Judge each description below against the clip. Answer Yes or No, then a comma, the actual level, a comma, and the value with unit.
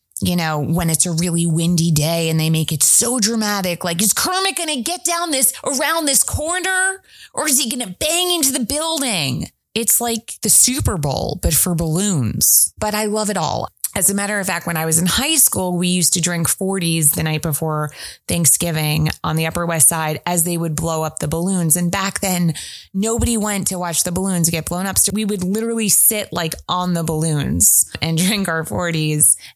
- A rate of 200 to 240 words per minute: Yes, fast, 205 wpm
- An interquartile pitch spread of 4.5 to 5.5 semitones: Yes, average, 5.1 semitones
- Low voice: No, medium, 180 Hz